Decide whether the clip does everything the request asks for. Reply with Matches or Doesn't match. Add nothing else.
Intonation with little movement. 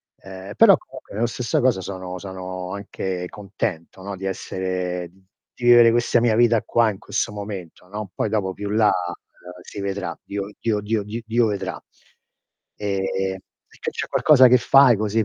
Doesn't match